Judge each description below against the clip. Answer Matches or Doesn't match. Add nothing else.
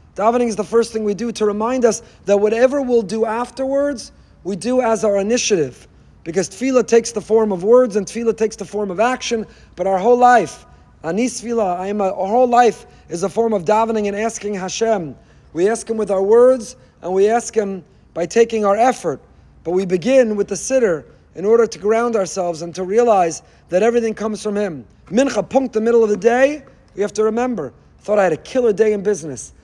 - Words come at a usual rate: Doesn't match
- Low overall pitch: Doesn't match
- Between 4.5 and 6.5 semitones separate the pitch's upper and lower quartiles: Doesn't match